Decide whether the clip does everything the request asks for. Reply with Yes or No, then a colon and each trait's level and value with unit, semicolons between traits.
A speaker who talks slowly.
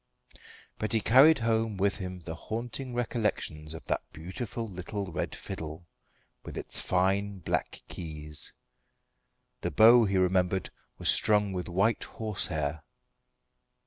Yes: slow, 125 wpm